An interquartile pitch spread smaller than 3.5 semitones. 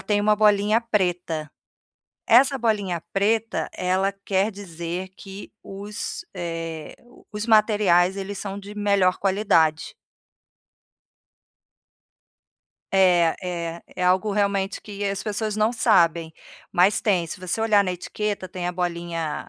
Yes: average, 3.0 semitones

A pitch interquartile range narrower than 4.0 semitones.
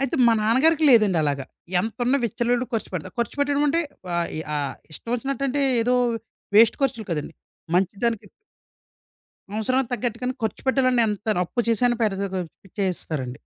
No: average, 4.8 semitones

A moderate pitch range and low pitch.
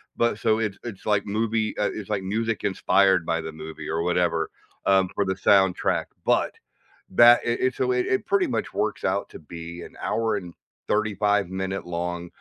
Yes: average, 4.0 semitones; low, 100 Hz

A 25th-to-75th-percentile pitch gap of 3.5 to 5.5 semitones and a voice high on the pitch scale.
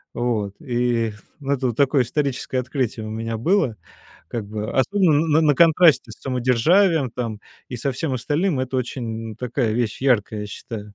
No: average, 3.8 semitones; low, 125 Hz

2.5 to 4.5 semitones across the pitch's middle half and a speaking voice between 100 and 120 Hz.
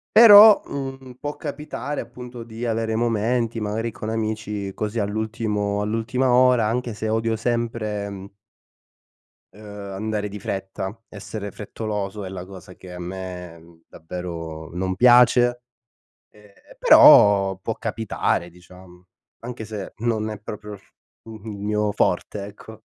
Yes: average, 2.9 semitones; low, 105 Hz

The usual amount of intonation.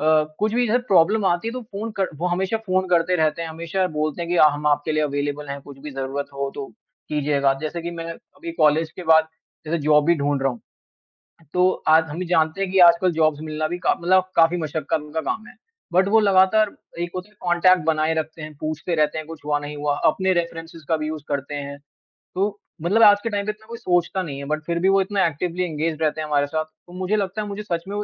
Yes: average, 3.5 semitones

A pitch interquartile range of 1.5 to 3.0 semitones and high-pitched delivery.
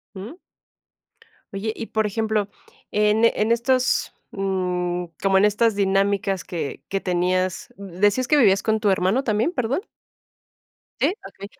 Yes: narrow, 2.6 semitones; high, 200 Hz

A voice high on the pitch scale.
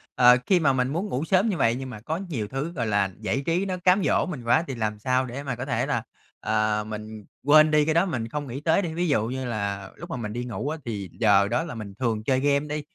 No: low, 130 Hz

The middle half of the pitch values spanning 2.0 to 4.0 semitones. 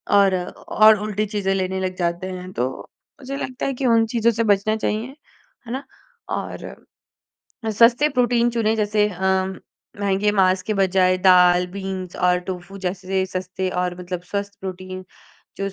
Yes: average, 2.8 semitones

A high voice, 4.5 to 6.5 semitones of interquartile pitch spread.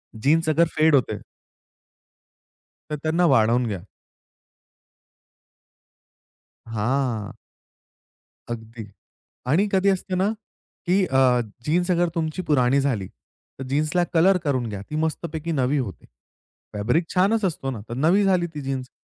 No: medium, 150 Hz; wide, 5.6 semitones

